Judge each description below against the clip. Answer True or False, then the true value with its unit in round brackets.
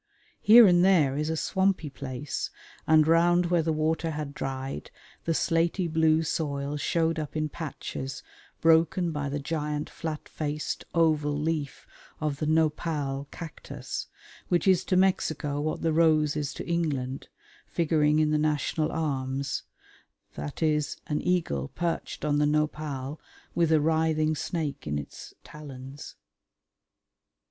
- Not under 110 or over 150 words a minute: True (135 wpm)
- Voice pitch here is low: False (155 Hz)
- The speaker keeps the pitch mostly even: True (2.2 semitones)